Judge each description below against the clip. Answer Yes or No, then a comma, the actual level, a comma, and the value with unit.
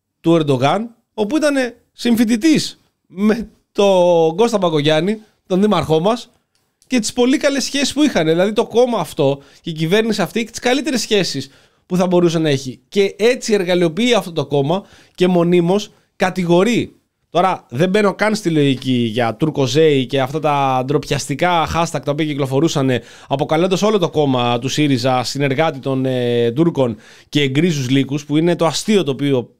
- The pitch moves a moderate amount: No, wide, 6.9 semitones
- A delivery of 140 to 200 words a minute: Yes, average, 165 wpm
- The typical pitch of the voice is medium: Yes, medium, 170 Hz